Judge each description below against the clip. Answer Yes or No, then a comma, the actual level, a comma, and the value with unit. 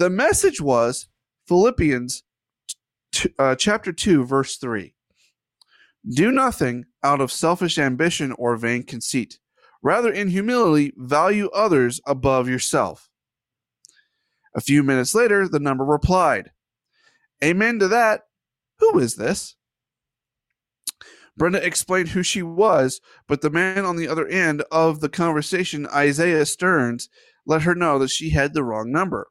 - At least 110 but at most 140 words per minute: Yes, slow, 135 wpm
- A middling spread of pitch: No, wide, 5.9 semitones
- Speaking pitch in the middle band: Yes, medium, 155 Hz